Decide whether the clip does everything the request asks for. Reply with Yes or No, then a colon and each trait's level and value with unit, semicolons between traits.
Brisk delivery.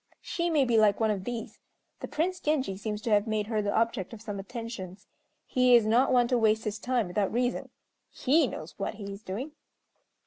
Yes: fast, 210 wpm